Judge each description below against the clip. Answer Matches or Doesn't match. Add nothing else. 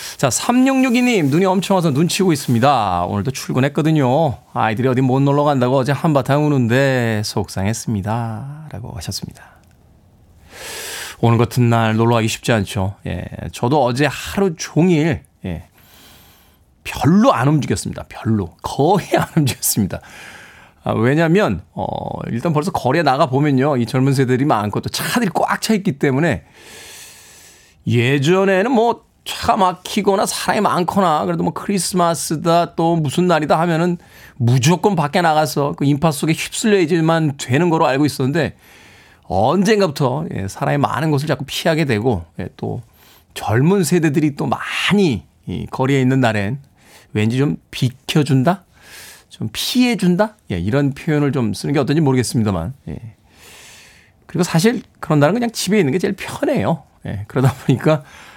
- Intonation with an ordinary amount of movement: Doesn't match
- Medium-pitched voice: Matches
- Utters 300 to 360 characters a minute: Matches